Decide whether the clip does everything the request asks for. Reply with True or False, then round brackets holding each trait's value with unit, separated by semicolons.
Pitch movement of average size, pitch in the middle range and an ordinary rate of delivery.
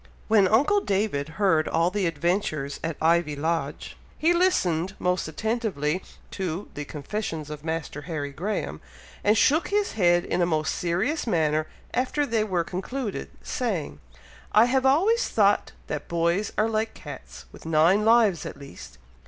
False (5.8 semitones; 180 Hz; 150 wpm)